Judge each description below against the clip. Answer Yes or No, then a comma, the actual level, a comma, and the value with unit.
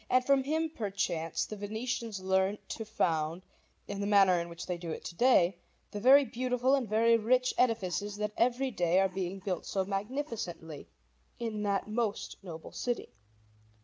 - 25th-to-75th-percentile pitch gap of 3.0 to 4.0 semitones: No, average, 4.5 semitones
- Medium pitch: No, high, 205 Hz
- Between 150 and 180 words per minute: Yes, average, 170 wpm